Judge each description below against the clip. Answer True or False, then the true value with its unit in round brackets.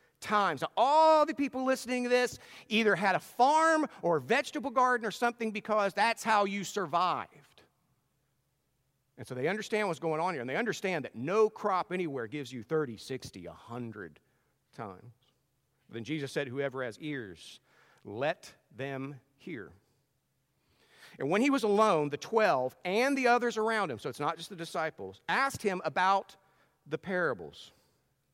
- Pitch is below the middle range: False (170 Hz)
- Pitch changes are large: True (8.3 semitones)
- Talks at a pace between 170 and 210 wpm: False (160 wpm)